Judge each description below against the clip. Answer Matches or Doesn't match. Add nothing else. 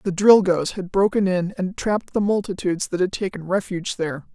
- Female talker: Matches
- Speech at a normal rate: Matches